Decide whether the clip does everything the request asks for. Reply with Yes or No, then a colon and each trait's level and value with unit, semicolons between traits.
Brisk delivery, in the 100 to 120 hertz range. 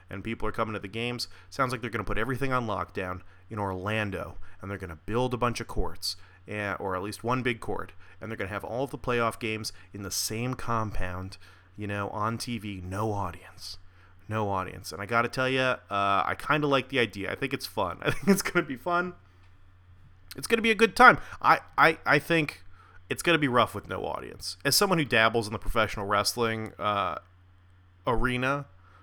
Yes: fast, 215 wpm; low, 105 Hz